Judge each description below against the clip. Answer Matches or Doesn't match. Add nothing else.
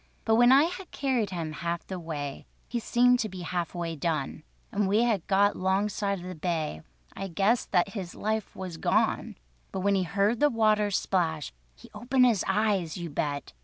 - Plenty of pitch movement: Doesn't match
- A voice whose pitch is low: Doesn't match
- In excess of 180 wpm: Matches